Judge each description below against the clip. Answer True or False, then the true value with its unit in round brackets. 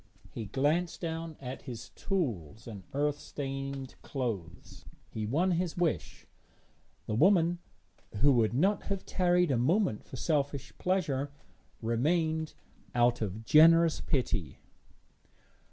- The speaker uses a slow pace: True (120 wpm)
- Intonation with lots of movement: True (6.0 semitones)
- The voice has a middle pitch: True (145 Hz)